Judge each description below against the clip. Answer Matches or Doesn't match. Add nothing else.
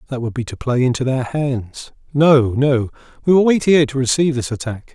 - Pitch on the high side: Doesn't match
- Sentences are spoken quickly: Matches